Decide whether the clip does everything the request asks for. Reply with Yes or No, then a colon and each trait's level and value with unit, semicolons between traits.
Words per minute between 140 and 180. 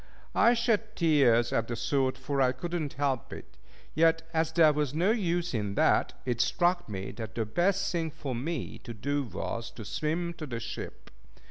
No: average, 195 wpm